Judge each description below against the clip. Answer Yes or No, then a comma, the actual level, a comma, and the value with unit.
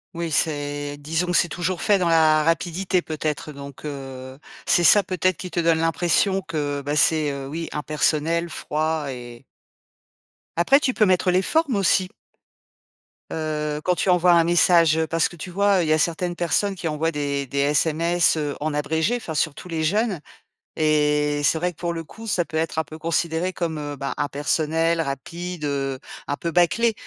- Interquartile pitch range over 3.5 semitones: No, average, 3.0 semitones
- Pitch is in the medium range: Yes, medium, 160 Hz